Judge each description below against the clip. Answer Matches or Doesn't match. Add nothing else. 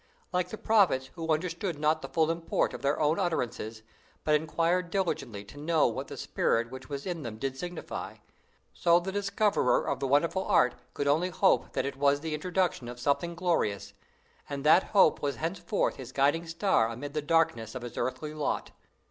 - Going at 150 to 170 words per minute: Doesn't match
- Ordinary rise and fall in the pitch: Matches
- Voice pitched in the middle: Matches